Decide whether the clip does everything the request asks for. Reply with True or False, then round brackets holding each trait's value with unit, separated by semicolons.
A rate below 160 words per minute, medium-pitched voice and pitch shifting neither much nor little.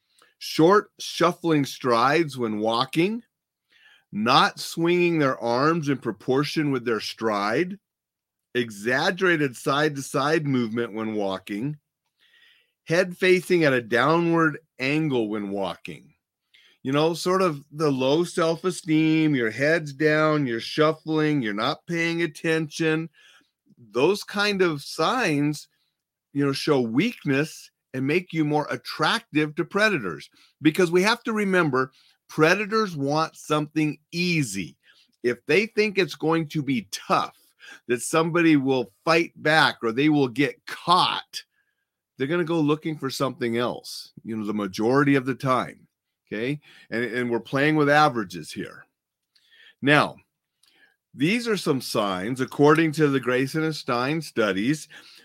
True (135 wpm; 155 Hz; 4.4 semitones)